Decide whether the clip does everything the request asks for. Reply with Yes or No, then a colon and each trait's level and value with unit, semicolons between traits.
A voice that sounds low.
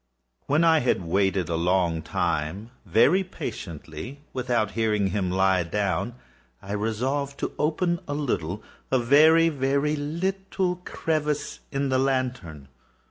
Yes: low, 125 Hz